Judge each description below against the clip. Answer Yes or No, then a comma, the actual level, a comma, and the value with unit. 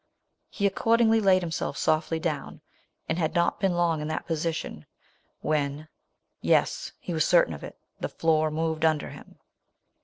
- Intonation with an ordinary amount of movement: No, narrow, 2.1 semitones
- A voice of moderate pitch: Yes, medium, 160 Hz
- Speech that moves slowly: No, average, 175 wpm